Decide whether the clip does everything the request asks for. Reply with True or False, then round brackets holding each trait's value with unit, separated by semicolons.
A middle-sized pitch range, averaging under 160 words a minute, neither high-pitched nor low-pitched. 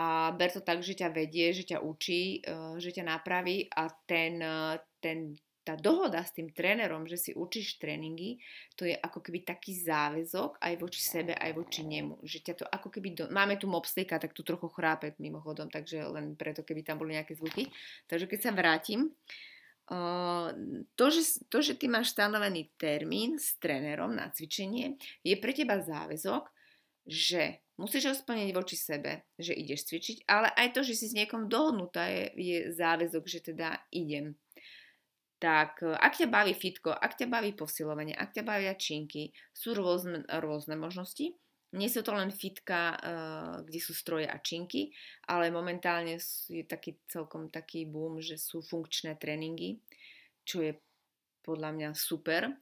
False (3.9 semitones; 165 wpm; 170 Hz)